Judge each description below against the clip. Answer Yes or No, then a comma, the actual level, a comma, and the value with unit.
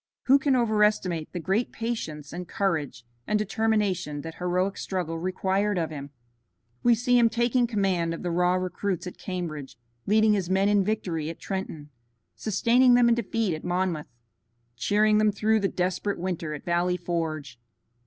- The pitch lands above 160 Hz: Yes, medium, 185 Hz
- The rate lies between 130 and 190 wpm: Yes, average, 165 wpm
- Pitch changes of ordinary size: Yes, average, 4.1 semitones